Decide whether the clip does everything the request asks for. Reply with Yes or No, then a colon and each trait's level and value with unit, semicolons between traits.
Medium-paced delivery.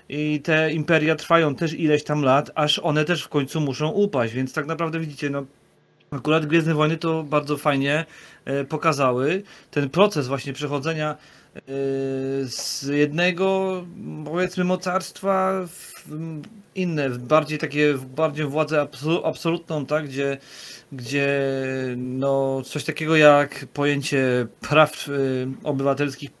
Yes: average, 125 wpm